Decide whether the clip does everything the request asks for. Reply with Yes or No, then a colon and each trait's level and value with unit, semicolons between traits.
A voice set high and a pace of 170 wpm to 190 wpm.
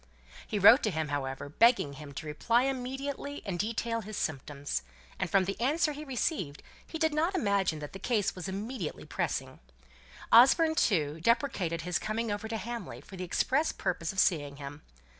Yes: high, 205 Hz; average, 180 wpm